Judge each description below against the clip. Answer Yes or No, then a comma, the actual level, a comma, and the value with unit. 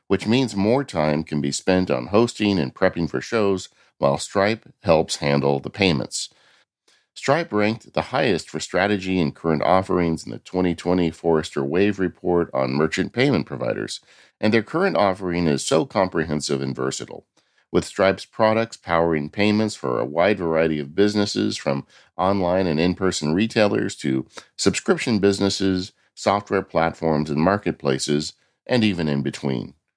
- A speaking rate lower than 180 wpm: Yes, average, 150 wpm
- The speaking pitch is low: Yes, very low, 90 Hz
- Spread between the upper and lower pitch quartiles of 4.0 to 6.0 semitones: Yes, average, 4.6 semitones